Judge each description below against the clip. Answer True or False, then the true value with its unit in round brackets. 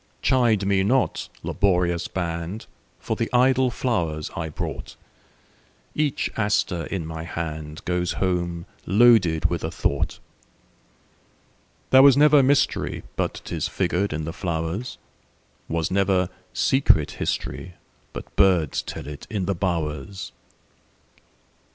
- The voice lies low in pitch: True (90 Hz)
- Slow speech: True (100 wpm)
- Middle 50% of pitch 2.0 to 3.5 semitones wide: False (4.8 semitones)